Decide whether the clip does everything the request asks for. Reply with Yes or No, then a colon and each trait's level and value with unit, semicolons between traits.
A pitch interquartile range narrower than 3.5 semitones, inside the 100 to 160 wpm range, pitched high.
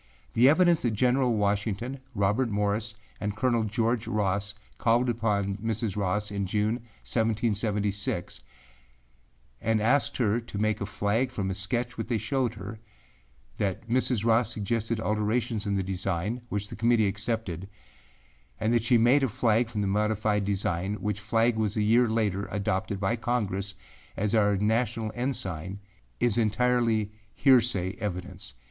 No: narrow, 2.6 semitones; average, 150 wpm; low, 110 Hz